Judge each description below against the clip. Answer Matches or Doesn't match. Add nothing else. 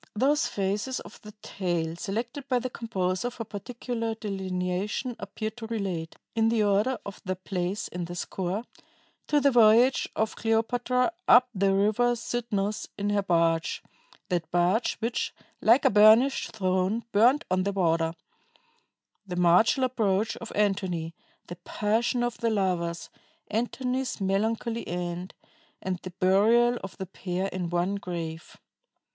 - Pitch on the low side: Doesn't match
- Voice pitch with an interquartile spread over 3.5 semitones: Matches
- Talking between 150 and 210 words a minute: Doesn't match